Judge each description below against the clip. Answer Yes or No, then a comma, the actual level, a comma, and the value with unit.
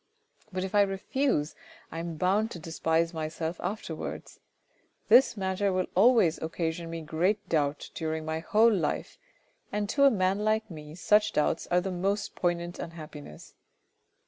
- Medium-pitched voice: Yes, medium, 180 Hz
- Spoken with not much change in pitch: No, average, 4.1 semitones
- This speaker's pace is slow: No, average, 155 wpm